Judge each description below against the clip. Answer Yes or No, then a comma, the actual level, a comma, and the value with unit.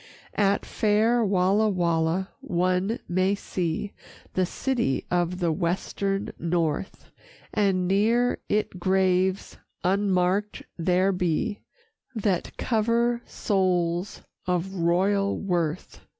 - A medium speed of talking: No, slow, 100 wpm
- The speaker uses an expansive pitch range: No, narrow, 2.5 semitones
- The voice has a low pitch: No, high, 190 Hz